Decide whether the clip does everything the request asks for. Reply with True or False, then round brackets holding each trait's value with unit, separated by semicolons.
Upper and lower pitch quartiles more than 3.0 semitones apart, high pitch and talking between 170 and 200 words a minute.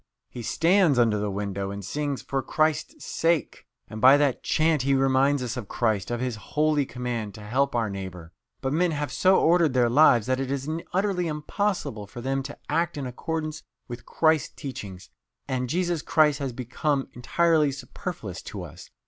False (4.5 semitones; 135 Hz; 180 wpm)